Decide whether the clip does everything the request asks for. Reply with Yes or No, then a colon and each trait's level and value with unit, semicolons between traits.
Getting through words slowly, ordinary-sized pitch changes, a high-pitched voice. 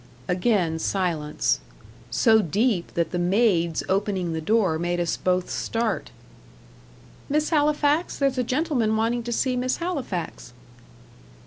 No: slow, 125 wpm; wide, 6.3 semitones; high, 215 Hz